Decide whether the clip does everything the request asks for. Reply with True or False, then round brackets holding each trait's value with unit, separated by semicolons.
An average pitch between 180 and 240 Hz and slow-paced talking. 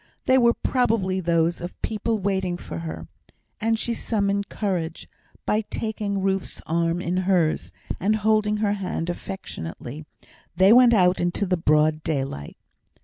False (190 Hz; 145 wpm)